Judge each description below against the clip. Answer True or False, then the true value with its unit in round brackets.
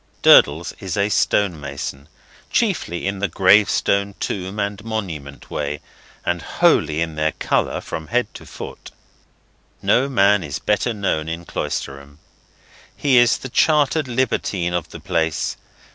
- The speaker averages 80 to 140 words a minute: True (135 wpm)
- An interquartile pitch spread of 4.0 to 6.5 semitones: True (5.2 semitones)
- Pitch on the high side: False (95 Hz)